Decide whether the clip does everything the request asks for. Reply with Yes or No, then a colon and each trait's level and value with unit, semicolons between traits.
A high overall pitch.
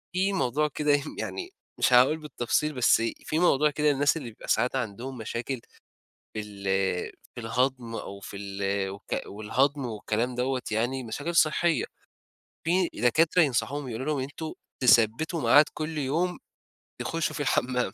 No: low, 130 Hz